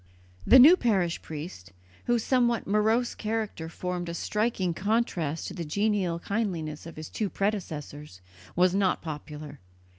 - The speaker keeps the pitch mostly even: No, average, 5.3 semitones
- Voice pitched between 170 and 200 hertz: Yes, medium, 185 Hz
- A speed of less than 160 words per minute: Yes, average, 140 wpm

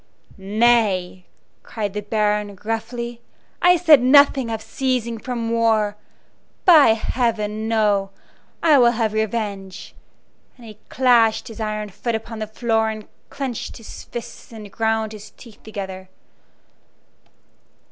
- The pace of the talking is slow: Yes, slow, 125 wpm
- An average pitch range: No, narrow, 2.1 semitones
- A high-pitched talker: Yes, high, 220 Hz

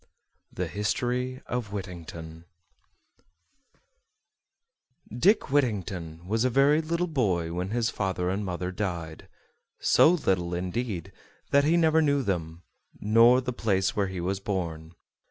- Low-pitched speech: Yes, low, 100 Hz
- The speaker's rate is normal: No, slow, 125 wpm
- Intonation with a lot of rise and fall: Yes, wide, 6.1 semitones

